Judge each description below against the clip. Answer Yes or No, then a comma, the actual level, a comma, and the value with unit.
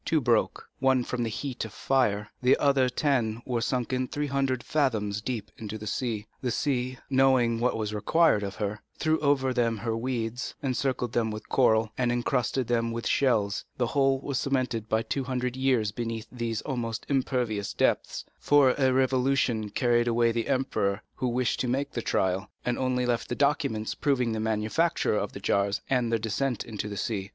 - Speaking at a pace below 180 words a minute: No, average, 185 wpm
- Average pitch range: Yes, average, 3.0 semitones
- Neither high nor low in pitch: No, low, 120 Hz